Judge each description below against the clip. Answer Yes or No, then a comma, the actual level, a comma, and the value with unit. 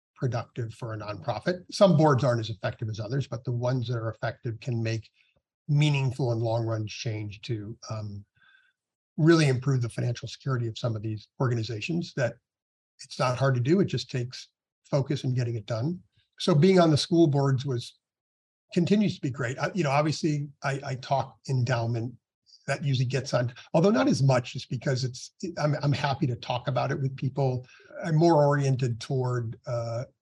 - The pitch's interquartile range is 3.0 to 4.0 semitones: Yes, average, 3.7 semitones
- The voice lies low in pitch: Yes, low, 130 Hz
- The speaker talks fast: No, average, 185 wpm